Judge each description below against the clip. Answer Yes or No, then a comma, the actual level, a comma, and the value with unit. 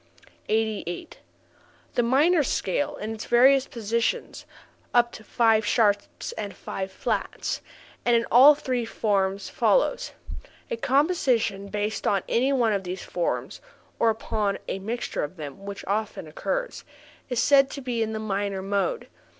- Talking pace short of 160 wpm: Yes, average, 145 wpm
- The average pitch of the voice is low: No, high, 220 Hz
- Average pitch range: Yes, average, 3.8 semitones